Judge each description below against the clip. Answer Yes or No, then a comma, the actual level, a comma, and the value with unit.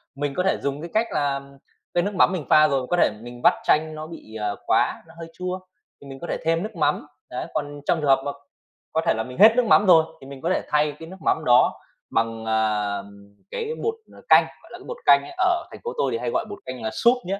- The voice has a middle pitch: Yes, medium, 150 Hz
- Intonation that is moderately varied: No, wide, 6.2 semitones